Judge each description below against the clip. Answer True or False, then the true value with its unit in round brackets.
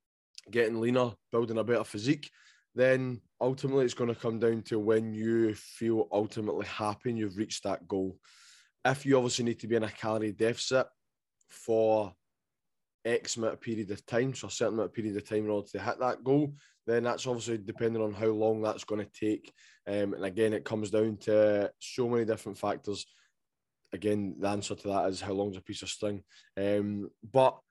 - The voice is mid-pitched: False (110 Hz)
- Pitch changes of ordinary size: False (2.3 semitones)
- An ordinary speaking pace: True (195 wpm)